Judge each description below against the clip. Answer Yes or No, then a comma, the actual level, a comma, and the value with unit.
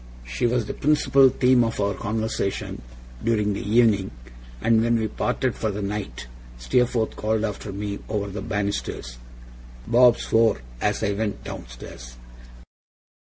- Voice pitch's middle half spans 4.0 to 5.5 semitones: No, narrow, 2.5 semitones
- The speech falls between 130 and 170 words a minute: Yes, average, 140 wpm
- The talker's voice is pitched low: Yes, low, 105 Hz